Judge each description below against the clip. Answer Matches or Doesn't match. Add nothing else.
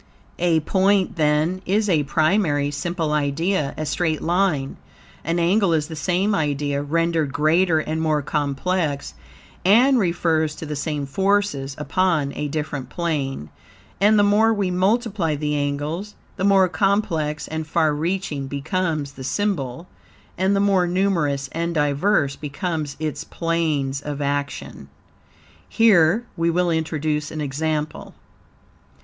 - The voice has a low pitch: Doesn't match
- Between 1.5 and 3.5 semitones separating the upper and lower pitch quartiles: Doesn't match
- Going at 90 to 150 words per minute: Matches